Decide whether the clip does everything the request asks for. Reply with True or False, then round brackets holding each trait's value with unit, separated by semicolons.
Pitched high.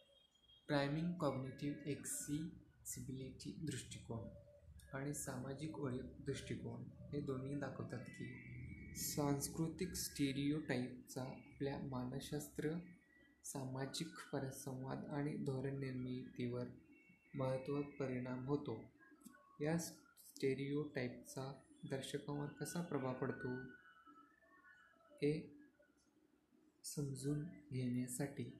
False (140 Hz)